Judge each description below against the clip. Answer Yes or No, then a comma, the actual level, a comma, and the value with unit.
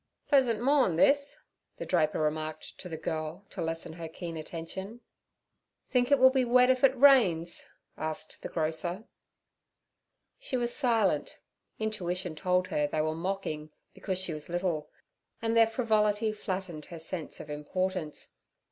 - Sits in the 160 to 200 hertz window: Yes, medium, 185 Hz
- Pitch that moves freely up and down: Yes, wide, 6.2 semitones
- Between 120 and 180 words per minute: Yes, average, 150 wpm